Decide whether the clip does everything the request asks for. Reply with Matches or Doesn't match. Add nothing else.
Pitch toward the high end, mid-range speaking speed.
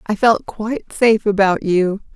Matches